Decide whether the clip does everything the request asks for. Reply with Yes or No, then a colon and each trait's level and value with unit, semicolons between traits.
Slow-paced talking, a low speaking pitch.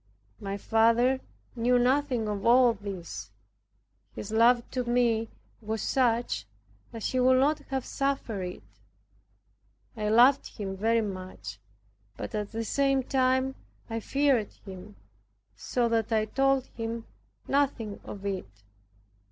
No: slow, 125 wpm; high, 230 Hz